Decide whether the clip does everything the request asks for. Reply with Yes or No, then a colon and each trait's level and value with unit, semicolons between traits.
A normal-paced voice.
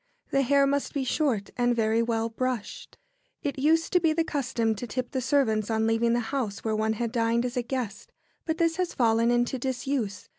No: fast, 210 wpm